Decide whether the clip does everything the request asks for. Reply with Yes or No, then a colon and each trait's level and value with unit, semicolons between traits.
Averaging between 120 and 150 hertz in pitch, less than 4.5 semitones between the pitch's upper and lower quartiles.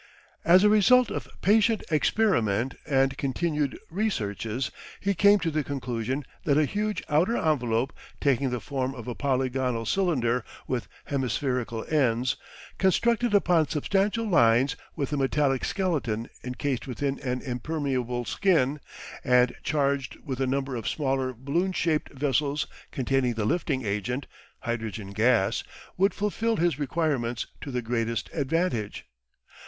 No: low, 135 Hz; average, 4.9 semitones